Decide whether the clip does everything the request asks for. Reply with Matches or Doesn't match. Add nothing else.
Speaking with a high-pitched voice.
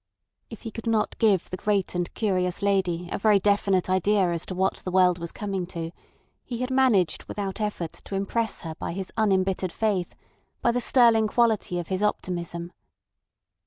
Matches